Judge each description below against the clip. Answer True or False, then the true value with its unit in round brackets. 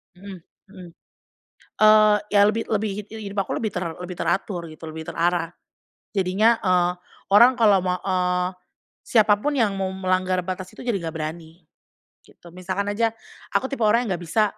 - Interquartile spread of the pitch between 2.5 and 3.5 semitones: True (2.9 semitones)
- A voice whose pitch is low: False (190 Hz)